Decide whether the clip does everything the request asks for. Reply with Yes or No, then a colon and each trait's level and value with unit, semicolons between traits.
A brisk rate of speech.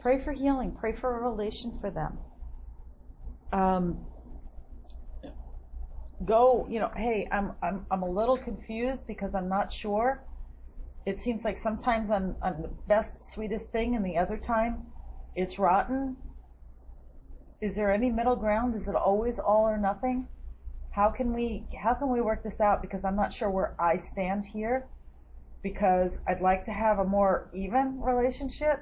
No: average, 160 wpm